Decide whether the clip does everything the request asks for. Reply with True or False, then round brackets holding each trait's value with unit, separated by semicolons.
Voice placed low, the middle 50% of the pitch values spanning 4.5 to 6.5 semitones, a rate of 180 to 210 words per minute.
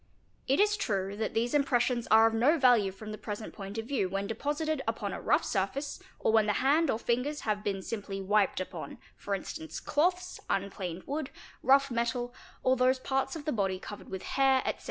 False (235 Hz; 5.2 semitones; 205 wpm)